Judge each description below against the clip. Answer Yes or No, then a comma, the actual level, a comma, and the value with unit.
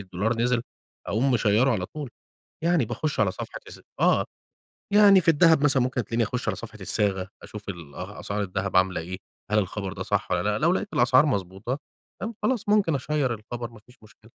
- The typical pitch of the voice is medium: No, low, 115 Hz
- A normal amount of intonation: No, wide, 5.8 semitones